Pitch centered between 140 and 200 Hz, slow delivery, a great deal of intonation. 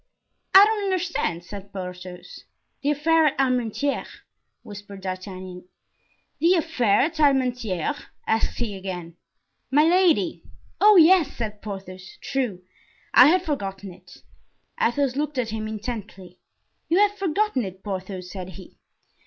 No: high, 230 Hz; slow, 125 wpm; wide, 8.2 semitones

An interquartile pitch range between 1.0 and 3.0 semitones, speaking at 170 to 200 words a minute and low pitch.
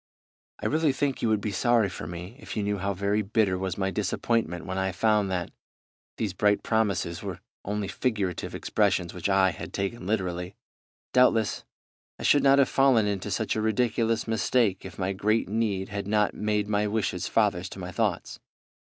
Yes: average, 2.7 semitones; average, 185 wpm; low, 105 Hz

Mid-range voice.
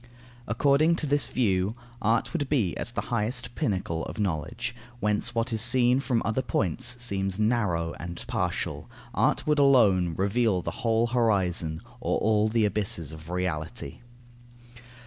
No: low, 110 Hz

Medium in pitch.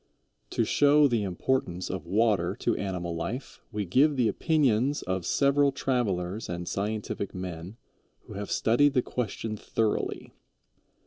No: low, 110 Hz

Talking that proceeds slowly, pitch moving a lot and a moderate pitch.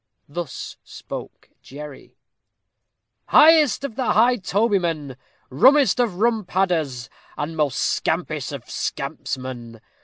Yes: slow, 95 wpm; wide, 8.6 semitones; medium, 175 Hz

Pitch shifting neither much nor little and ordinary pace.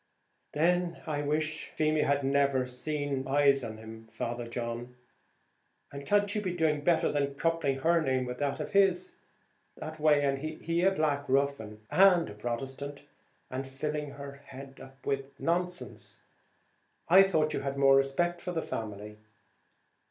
Yes: average, 3.3 semitones; average, 155 wpm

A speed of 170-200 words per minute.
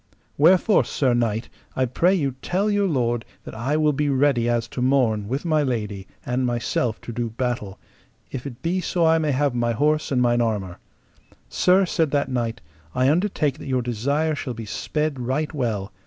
Yes: average, 190 wpm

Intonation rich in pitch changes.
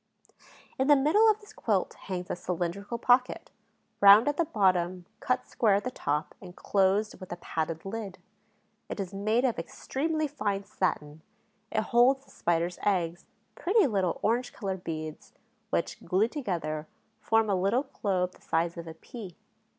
Yes: wide, 5.7 semitones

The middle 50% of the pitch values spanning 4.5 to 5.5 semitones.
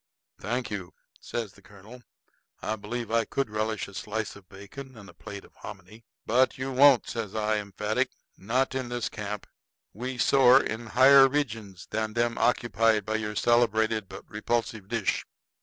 No: average, 2.7 semitones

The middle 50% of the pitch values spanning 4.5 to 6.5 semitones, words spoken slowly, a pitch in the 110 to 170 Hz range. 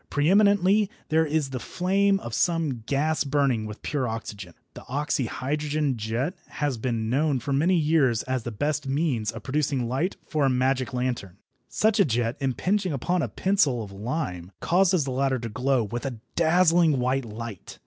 No: average, 4.9 semitones; average, 180 wpm; low, 135 Hz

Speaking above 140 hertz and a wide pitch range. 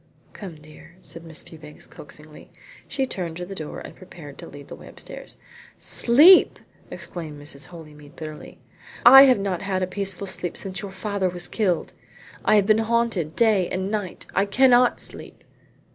No: medium, 185 Hz; average, 4.8 semitones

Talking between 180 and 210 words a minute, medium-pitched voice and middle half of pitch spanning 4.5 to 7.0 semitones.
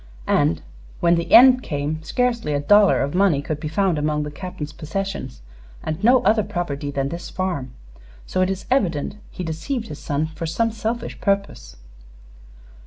No: average, 170 wpm; medium, 170 Hz; average, 5.2 semitones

